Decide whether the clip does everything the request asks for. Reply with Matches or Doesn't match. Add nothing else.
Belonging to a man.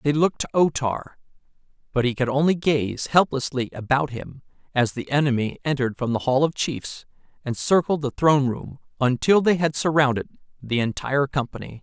Matches